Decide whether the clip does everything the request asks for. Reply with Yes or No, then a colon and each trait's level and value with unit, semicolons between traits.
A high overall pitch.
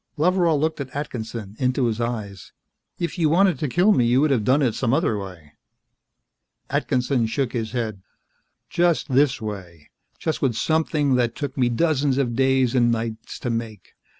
No: low, 125 Hz